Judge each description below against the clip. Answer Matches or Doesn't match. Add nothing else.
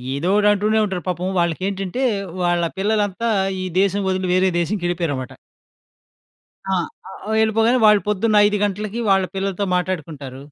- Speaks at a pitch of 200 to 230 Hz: Doesn't match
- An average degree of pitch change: Matches